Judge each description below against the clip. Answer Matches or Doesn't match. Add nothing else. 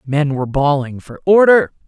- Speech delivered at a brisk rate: Doesn't match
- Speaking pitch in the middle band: Matches